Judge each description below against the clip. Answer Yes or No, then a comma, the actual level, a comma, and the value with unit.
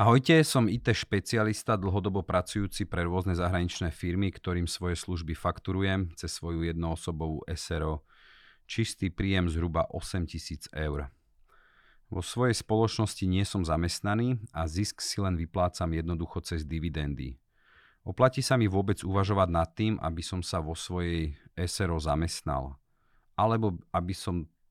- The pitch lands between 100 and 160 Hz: No, very low, 90 Hz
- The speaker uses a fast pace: No, average, 130 wpm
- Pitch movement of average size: Yes, average, 3.6 semitones